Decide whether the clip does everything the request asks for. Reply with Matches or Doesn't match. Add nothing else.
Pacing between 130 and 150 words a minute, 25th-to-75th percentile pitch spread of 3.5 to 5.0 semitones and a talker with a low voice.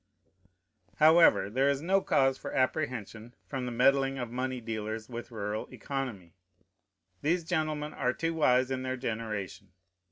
Matches